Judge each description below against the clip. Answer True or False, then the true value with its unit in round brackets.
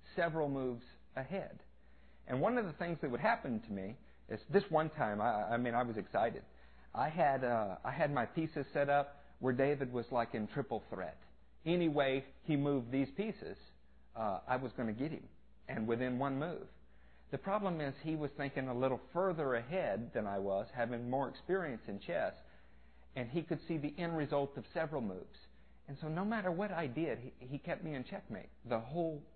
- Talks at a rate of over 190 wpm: True (200 wpm)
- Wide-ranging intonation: True (5.9 semitones)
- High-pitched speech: False (135 Hz)